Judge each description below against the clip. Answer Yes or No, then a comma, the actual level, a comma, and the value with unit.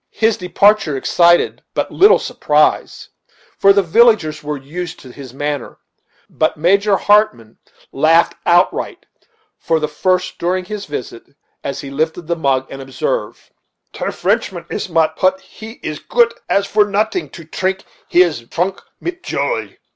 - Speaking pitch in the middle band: Yes, medium, 175 Hz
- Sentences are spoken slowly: No, average, 150 wpm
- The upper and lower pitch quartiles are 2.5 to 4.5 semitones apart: No, average, 5.1 semitones